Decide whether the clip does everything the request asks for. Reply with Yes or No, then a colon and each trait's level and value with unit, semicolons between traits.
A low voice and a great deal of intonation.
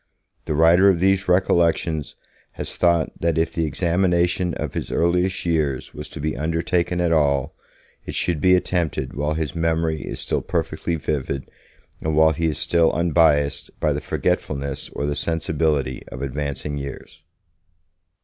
No: very low, 80 Hz; average, 2.8 semitones